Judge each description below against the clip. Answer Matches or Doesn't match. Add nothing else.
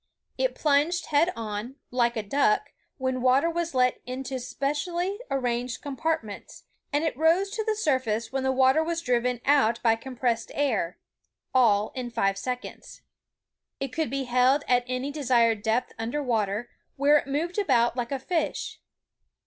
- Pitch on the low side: Doesn't match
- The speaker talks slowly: Doesn't match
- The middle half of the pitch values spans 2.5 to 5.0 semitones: Matches